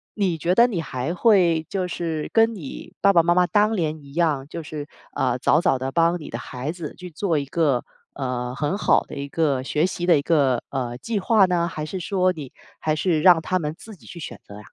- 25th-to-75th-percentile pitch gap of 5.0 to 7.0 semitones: No, average, 4.2 semitones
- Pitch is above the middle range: No, medium, 165 Hz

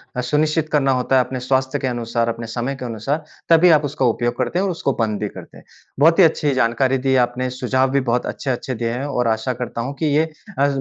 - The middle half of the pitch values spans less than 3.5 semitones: Yes, average, 2.9 semitones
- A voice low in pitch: Yes, low, 130 Hz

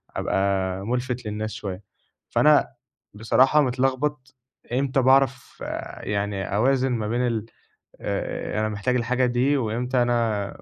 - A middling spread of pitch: Yes, average, 3.3 semitones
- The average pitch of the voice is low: Yes, low, 120 Hz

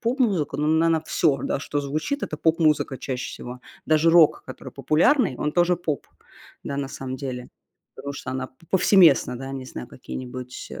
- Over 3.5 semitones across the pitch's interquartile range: Yes, average, 4.1 semitones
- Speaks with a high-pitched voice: No, medium, 150 Hz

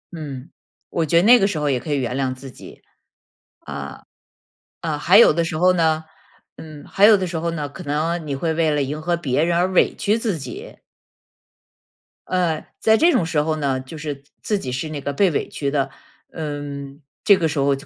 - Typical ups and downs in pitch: Yes, average, 3.3 semitones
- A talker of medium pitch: Yes, medium, 155 Hz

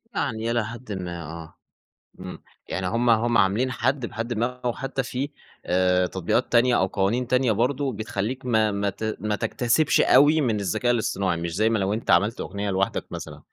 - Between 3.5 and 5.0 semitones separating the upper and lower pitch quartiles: Yes, average, 4.1 semitones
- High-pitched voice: No, low, 110 Hz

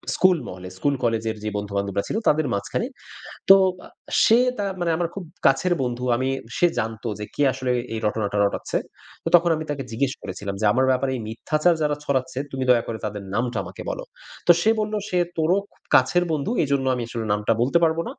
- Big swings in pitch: Yes, wide, 6.2 semitones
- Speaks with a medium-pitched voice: No, low, 130 Hz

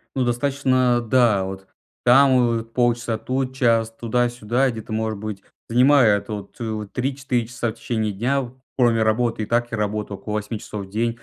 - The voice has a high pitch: No, low, 115 Hz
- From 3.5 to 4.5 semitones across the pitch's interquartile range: No, narrow, 2.5 semitones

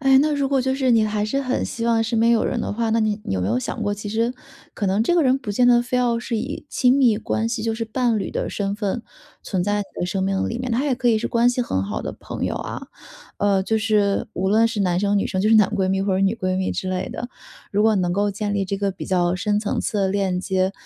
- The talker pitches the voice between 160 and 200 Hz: No, high, 215 Hz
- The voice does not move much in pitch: No, average, 3.3 semitones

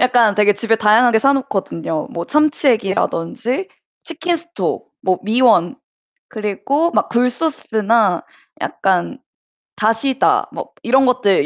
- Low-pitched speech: No, high, 230 Hz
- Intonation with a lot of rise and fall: No, average, 4.8 semitones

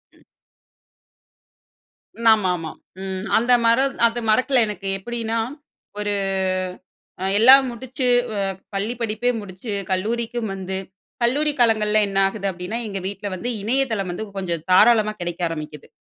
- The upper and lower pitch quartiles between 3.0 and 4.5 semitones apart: Yes, average, 3.8 semitones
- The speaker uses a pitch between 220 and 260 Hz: No, high, 210 Hz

